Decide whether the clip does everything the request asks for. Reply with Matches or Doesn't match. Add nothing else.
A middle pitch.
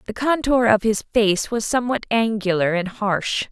Doesn't match